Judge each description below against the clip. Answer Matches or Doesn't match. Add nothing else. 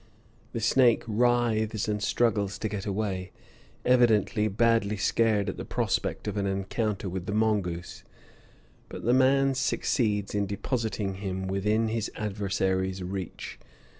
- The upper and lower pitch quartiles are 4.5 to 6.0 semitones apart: Doesn't match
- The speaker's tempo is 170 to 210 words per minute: Doesn't match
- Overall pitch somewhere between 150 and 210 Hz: Doesn't match